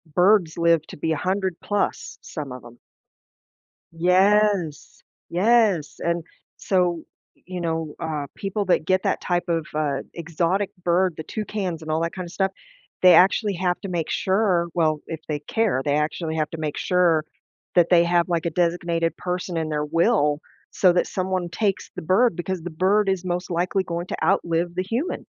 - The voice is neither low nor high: Yes, medium, 175 Hz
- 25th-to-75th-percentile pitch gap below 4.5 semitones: Yes, narrow, 2.5 semitones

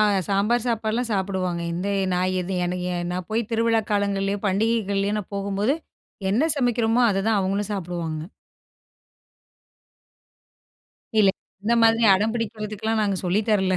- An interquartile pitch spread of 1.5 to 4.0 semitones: Yes, average, 2.8 semitones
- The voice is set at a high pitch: Yes, high, 205 Hz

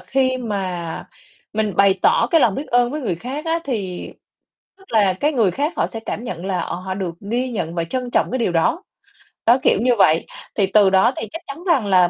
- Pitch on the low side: No, high, 220 Hz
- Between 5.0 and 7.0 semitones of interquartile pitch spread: Yes, wide, 5.6 semitones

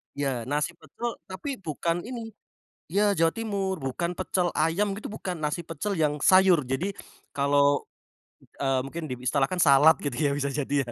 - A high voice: No, medium, 160 Hz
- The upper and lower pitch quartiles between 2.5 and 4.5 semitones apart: No, average, 5.0 semitones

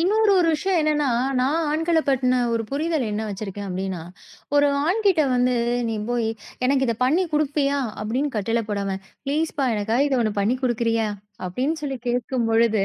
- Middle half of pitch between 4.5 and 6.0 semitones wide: Yes, average, 5.2 semitones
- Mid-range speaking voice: No, very high, 255 Hz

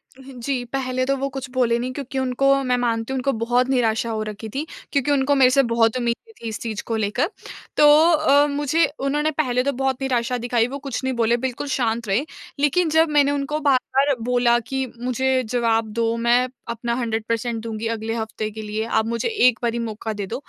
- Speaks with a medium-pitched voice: No, very high, 250 Hz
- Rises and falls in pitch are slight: No, average, 3.0 semitones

